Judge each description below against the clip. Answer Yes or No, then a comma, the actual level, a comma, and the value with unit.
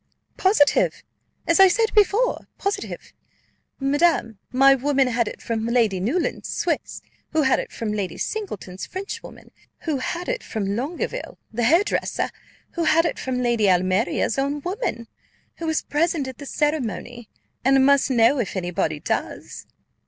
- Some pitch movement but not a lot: No, wide, 6.5 semitones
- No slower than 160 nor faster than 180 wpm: No, average, 150 wpm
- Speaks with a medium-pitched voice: No, very high, 270 Hz